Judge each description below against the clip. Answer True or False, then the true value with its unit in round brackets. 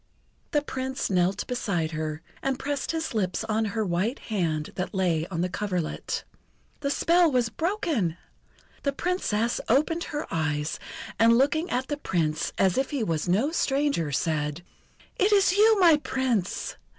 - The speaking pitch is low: False (225 Hz)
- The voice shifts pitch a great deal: True (8.8 semitones)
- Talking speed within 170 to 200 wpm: False (155 wpm)